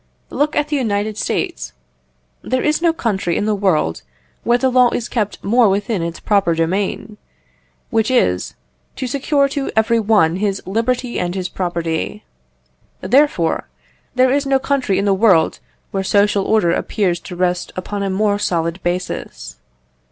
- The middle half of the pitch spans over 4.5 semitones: Yes, average, 5.3 semitones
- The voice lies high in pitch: Yes, high, 205 Hz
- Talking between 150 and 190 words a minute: Yes, average, 160 wpm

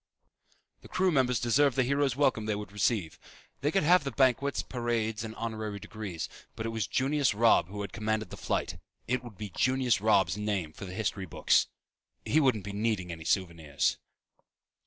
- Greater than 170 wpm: Yes, average, 180 wpm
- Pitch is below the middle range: Yes, low, 110 Hz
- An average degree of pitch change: Yes, average, 4.2 semitones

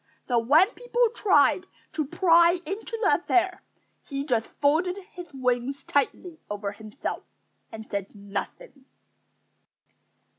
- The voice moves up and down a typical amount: No, wide, 7.4 semitones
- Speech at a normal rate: No, slow, 115 wpm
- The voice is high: Yes, very high, 290 Hz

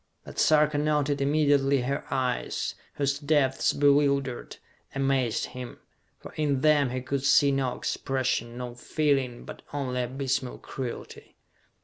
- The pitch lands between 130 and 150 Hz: Yes, low, 135 Hz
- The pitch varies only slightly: Yes, narrow, 2.1 semitones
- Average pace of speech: No, slow, 125 wpm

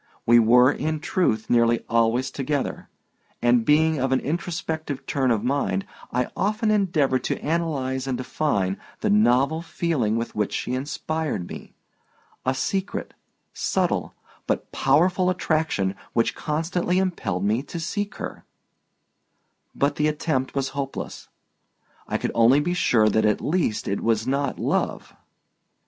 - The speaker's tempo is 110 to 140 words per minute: Yes, slow, 135 wpm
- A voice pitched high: No, medium, 140 Hz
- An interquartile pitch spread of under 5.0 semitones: No, average, 5.3 semitones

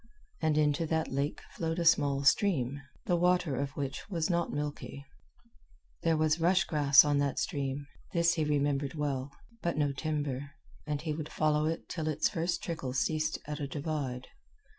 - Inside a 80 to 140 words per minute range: No, average, 170 wpm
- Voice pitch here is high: No, medium, 150 Hz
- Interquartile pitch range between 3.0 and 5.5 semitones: No, narrow, 2.5 semitones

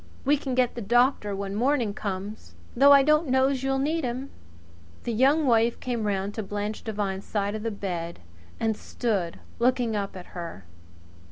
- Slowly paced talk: No, average, 175 wpm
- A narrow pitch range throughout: No, average, 4.6 semitones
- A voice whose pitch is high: Yes, high, 225 Hz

